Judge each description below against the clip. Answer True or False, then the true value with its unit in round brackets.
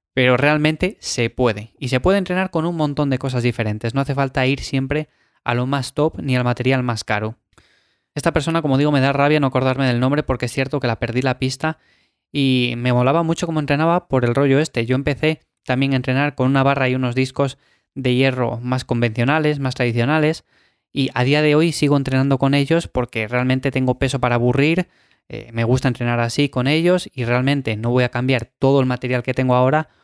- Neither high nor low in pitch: False (130 Hz)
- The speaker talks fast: True (215 wpm)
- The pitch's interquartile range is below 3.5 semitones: True (2.8 semitones)